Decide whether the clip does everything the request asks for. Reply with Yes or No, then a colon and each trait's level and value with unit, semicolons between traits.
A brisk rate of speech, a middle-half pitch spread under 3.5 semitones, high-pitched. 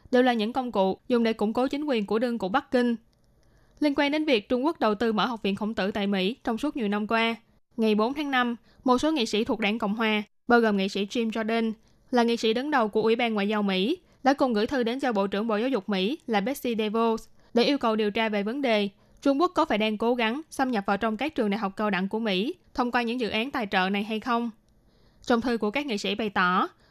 Yes: fast, 280 wpm; average, 3.0 semitones; high, 225 Hz